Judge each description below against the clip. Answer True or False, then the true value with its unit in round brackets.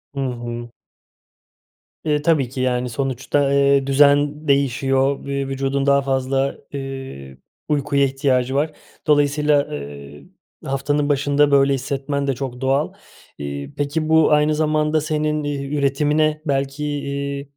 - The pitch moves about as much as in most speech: False (1.5 semitones)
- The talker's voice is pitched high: False (140 Hz)